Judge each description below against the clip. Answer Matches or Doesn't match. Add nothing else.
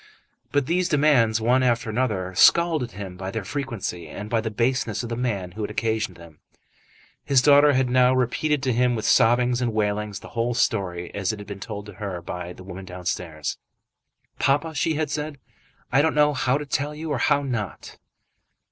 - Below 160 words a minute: Doesn't match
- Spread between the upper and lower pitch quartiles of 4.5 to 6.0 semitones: Matches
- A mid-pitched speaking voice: Doesn't match